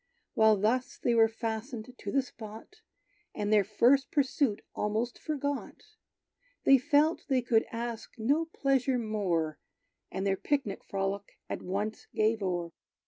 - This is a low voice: No, high, 225 Hz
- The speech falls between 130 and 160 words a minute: Yes, average, 140 wpm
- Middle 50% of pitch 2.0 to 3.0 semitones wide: No, average, 4.3 semitones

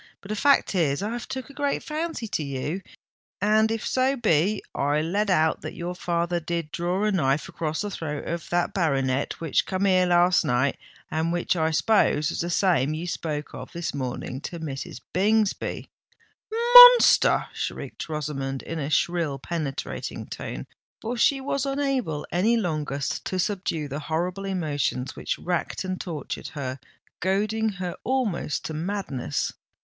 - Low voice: No, medium, 175 Hz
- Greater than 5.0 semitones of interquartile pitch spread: Yes, wide, 5.4 semitones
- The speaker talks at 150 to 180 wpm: Yes, average, 160 wpm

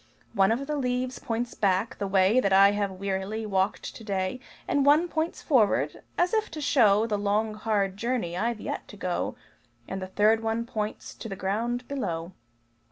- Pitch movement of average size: Yes, average, 4.0 semitones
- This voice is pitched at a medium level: No, high, 215 Hz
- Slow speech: No, average, 180 wpm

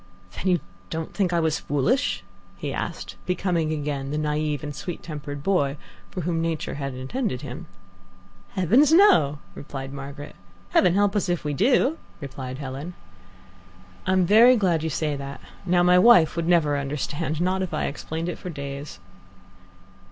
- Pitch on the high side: No, medium, 160 Hz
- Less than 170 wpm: Yes, average, 160 wpm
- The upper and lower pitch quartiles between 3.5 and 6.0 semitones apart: Yes, average, 4.0 semitones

